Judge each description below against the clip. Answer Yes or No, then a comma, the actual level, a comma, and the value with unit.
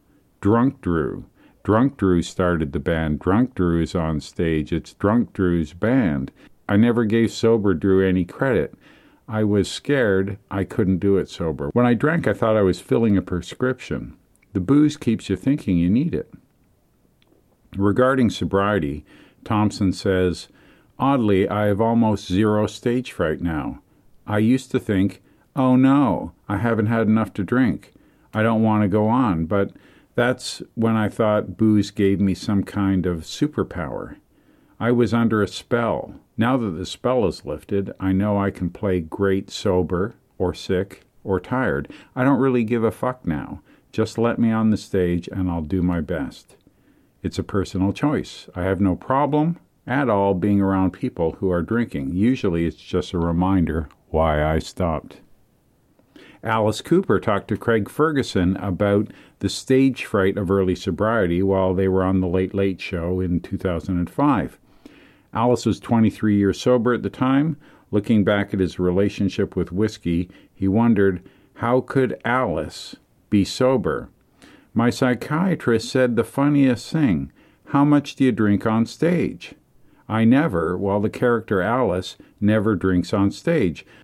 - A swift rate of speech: No, average, 160 wpm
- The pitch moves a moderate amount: Yes, average, 3.9 semitones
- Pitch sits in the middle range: No, low, 100 Hz